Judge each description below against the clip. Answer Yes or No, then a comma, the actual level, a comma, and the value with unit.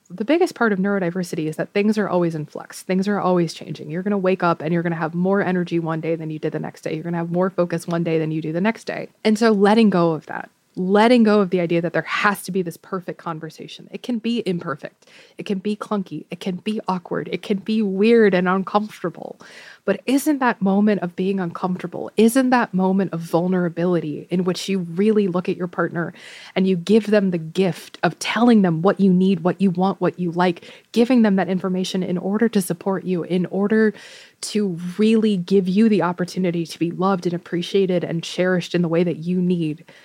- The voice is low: No, medium, 185 Hz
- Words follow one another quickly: Yes, fast, 230 wpm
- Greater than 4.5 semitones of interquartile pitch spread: No, average, 3.1 semitones